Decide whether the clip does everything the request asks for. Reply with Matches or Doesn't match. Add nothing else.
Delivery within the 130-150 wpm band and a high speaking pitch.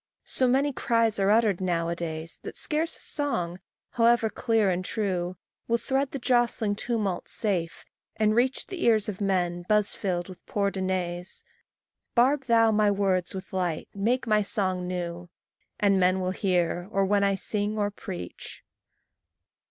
Doesn't match